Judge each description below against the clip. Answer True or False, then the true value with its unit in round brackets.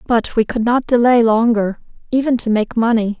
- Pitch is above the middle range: True (230 Hz)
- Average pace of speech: True (190 wpm)